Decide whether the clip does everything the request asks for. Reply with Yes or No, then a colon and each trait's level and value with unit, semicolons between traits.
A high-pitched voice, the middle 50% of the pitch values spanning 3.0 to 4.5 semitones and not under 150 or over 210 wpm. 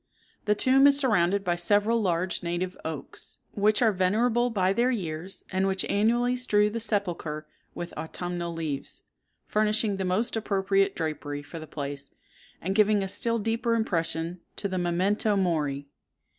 Yes: high, 195 Hz; average, 4.1 semitones; average, 155 wpm